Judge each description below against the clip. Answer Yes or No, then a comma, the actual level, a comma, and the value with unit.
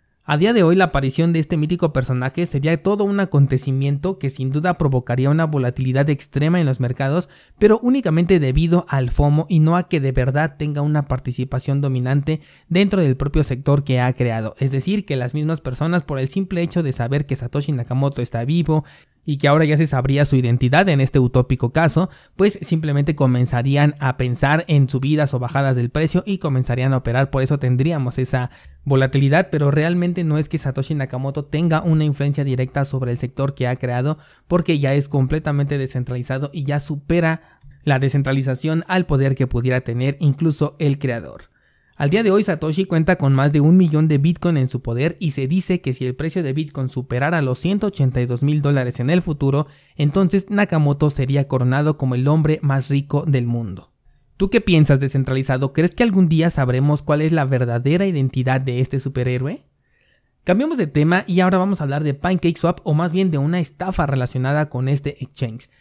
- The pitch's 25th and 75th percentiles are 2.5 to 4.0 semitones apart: Yes, average, 3.7 semitones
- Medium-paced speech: No, fast, 195 wpm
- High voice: No, medium, 145 Hz